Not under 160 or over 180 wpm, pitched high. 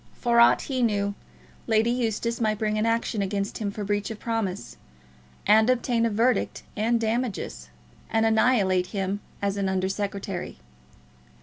No: average, 150 wpm; high, 215 Hz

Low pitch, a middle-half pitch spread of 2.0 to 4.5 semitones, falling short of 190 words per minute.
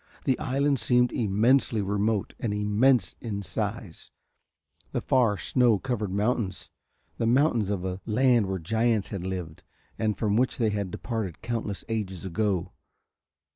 Yes: low, 110 Hz; average, 3.3 semitones; average, 140 wpm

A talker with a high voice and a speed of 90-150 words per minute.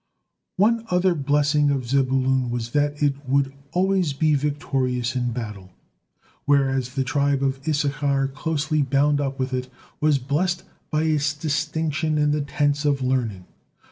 No: medium, 140 Hz; average, 145 wpm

